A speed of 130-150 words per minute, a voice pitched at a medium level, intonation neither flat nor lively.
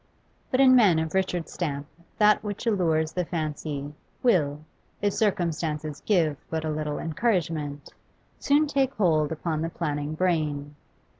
Yes: average, 140 wpm; medium, 160 Hz; average, 4.0 semitones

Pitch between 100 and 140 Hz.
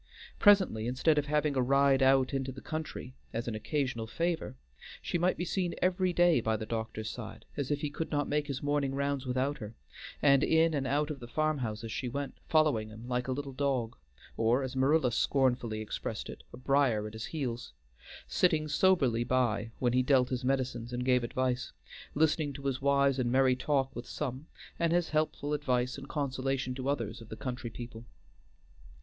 Yes: low, 135 Hz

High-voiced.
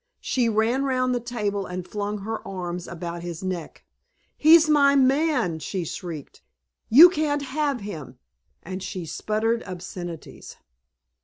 Yes: high, 210 Hz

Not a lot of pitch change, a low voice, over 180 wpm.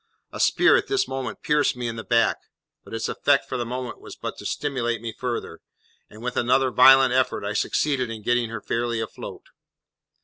Yes: narrow, 2.1 semitones; low, 120 Hz; average, 200 wpm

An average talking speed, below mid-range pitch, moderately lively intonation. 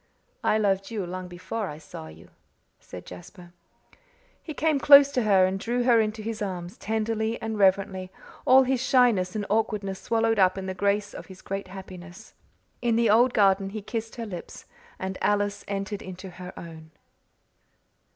No: average, 170 wpm; high, 200 Hz; average, 3.3 semitones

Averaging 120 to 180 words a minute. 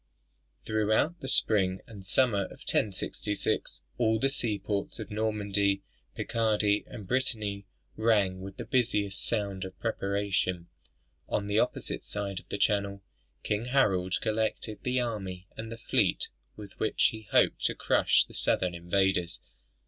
Yes: average, 140 wpm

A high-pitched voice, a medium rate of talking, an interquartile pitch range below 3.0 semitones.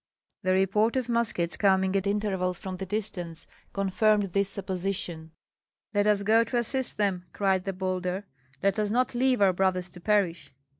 Yes: high, 195 Hz; average, 165 wpm; narrow, 2.4 semitones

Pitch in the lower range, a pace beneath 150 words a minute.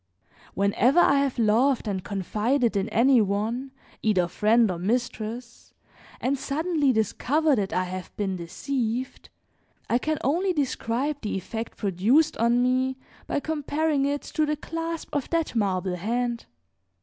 No: high, 245 Hz; average, 140 wpm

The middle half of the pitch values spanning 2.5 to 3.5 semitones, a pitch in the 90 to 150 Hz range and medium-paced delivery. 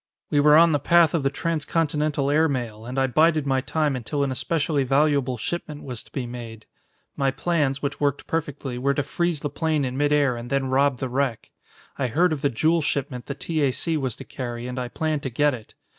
No: average, 2.9 semitones; medium, 140 Hz; fast, 225 wpm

